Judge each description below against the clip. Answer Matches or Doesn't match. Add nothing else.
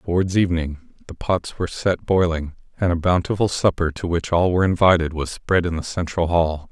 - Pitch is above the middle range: Doesn't match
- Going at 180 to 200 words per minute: Matches